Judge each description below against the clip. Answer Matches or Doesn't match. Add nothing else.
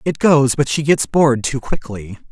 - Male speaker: Matches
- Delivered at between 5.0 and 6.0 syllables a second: Doesn't match